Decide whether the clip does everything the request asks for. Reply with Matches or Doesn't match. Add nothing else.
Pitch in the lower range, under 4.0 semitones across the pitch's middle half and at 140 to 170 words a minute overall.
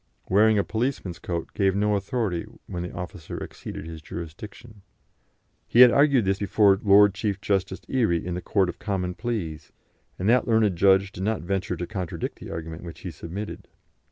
Doesn't match